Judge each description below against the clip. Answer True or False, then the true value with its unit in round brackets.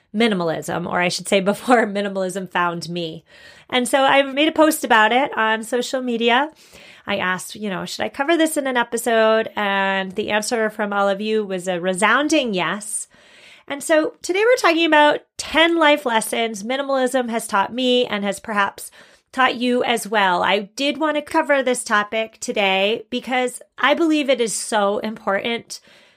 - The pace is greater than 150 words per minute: True (175 wpm)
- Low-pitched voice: False (230 Hz)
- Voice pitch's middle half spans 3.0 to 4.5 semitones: False (5.2 semitones)